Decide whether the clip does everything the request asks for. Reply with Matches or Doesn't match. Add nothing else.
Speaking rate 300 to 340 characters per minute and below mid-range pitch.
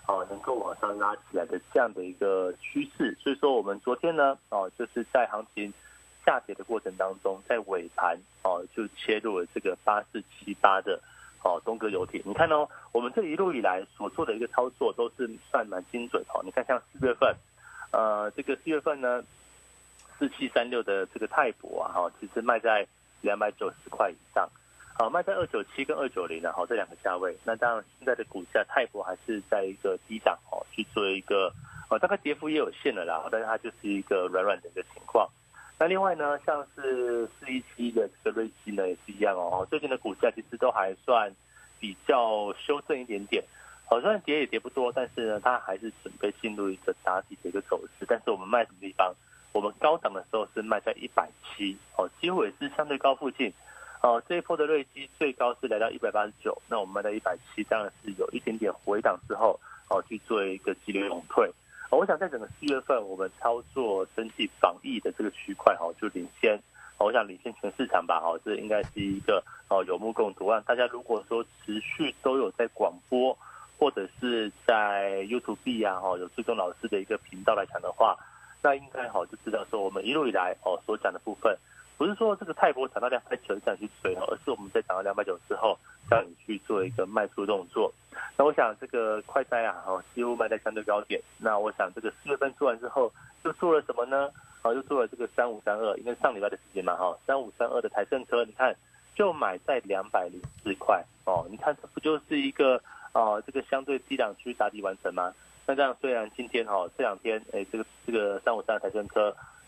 Matches